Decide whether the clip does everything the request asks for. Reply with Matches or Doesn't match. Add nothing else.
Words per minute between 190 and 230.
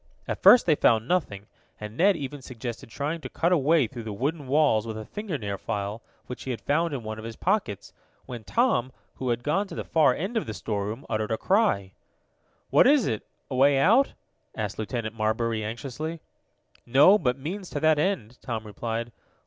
Matches